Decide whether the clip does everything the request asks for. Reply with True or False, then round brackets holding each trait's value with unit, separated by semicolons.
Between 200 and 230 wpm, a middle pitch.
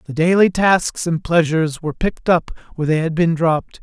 True (205 wpm; 165 Hz)